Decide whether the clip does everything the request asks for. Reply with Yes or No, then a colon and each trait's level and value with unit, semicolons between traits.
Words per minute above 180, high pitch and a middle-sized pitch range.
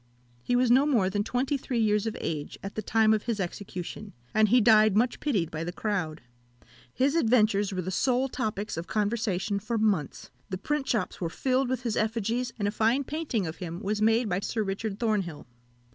Yes: fast, 205 wpm; high, 215 Hz; average, 3.7 semitones